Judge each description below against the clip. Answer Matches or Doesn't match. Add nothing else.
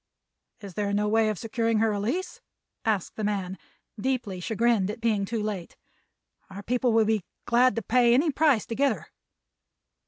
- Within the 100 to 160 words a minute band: Doesn't match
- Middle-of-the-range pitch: Doesn't match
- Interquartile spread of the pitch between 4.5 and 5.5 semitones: Doesn't match